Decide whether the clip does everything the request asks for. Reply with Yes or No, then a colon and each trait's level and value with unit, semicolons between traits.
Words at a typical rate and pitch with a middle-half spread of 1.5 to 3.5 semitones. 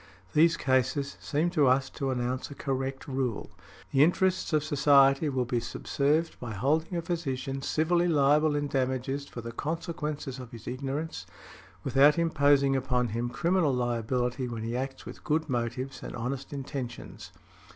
Yes: average, 155 wpm; average, 3.1 semitones